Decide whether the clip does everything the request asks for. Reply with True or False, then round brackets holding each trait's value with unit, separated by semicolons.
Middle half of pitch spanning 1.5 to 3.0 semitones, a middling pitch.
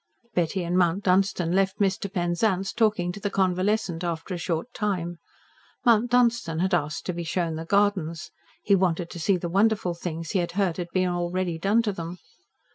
True (2.7 semitones; 180 Hz)